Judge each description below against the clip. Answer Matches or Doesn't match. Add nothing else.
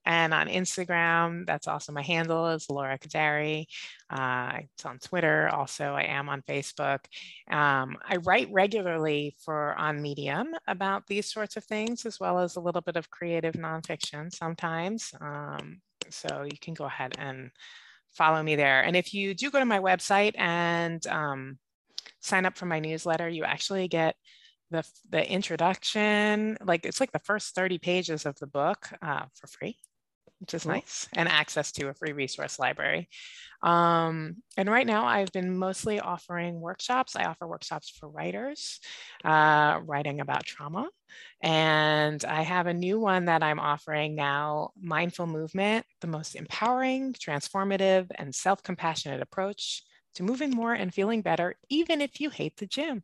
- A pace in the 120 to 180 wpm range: Matches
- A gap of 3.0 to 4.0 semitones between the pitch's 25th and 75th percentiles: Doesn't match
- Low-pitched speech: Doesn't match